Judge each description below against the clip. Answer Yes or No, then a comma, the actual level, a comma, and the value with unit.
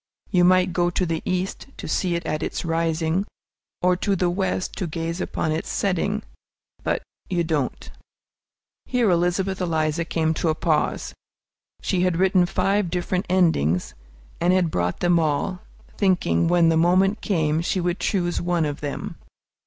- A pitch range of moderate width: No, narrow, 2.3 semitones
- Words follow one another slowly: No, average, 160 wpm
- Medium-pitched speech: Yes, medium, 175 Hz